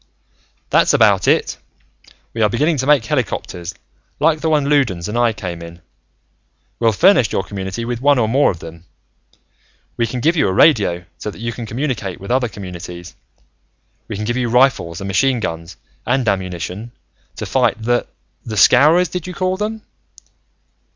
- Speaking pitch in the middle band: No, low, 115 Hz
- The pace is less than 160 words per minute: No, average, 170 wpm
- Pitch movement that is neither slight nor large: No, wide, 6.6 semitones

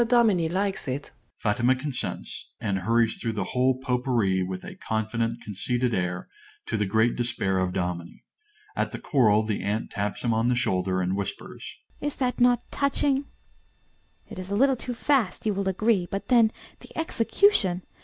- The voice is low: Yes, low, 125 Hz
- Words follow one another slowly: No, average, 175 wpm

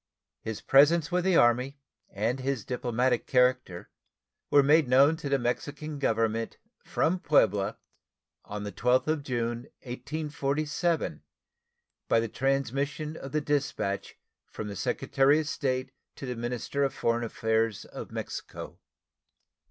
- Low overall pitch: Yes, low, 130 Hz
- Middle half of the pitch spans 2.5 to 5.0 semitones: Yes, average, 3.8 semitones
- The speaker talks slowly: Yes, slow, 130 wpm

